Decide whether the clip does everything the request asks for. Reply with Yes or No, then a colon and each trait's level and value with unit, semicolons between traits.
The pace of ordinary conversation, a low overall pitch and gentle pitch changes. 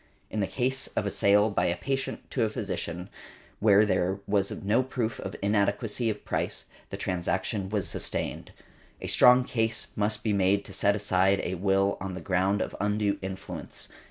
Yes: average, 180 wpm; low, 100 Hz; narrow, 2.2 semitones